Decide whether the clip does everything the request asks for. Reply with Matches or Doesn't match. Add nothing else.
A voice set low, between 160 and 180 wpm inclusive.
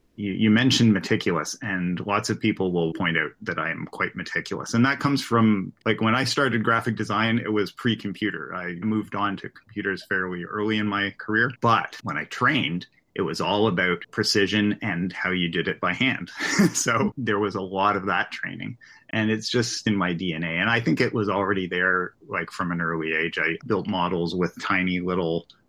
Doesn't match